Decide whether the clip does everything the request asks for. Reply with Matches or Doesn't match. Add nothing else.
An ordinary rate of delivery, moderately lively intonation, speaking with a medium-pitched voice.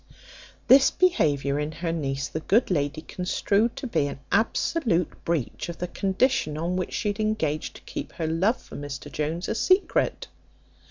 Doesn't match